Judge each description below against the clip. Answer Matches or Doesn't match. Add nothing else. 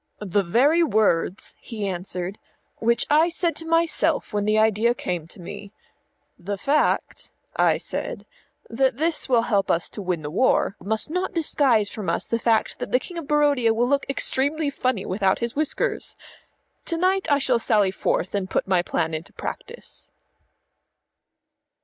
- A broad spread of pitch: Matches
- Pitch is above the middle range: Matches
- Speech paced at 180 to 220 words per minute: Doesn't match